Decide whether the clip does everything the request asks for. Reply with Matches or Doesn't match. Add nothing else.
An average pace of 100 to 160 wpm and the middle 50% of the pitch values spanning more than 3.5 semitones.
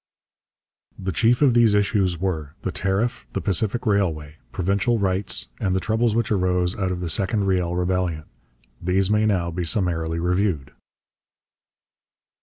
Doesn't match